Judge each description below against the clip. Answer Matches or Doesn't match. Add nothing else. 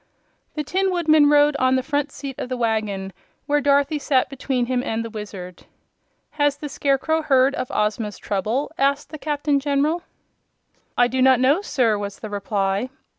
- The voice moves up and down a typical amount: Matches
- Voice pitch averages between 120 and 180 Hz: Doesn't match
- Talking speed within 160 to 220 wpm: Matches